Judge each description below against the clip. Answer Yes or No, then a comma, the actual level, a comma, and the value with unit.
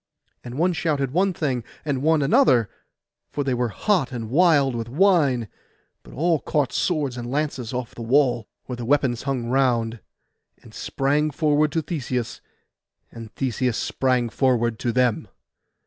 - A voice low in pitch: Yes, low, 130 Hz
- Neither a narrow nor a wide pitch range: Yes, average, 3.7 semitones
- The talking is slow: No, average, 155 wpm